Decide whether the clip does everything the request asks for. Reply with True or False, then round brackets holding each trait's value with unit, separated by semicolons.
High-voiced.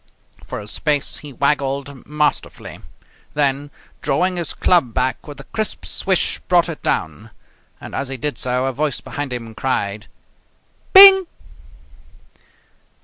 False (140 Hz)